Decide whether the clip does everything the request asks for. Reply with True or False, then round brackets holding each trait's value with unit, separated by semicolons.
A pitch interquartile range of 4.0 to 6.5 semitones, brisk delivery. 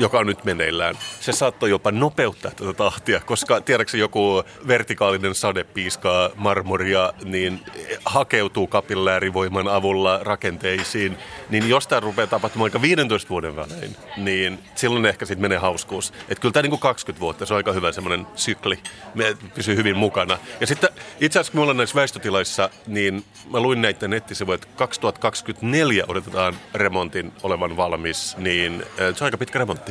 False (3.3 semitones; 160 wpm)